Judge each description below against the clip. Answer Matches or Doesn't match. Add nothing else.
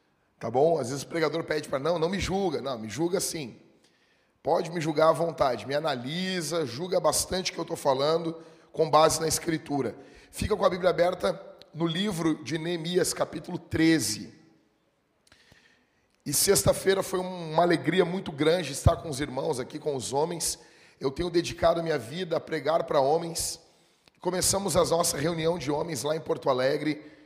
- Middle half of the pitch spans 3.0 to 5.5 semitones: Doesn't match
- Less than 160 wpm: Doesn't match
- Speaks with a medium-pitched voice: Matches